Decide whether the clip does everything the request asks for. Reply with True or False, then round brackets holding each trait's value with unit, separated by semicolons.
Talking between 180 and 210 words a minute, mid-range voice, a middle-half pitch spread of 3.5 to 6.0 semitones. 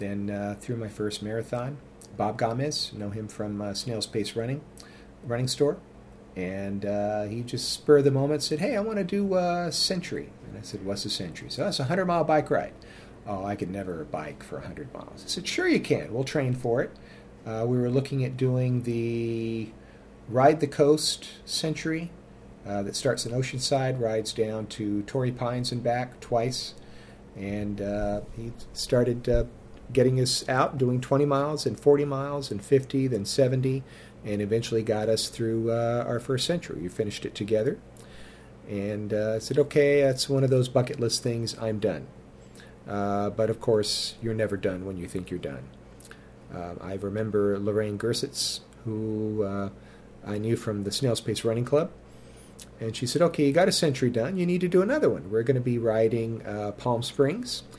False (190 wpm; 115 Hz; 4.6 semitones)